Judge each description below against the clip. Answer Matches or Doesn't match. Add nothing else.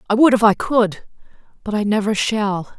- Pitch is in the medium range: Doesn't match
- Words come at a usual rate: Matches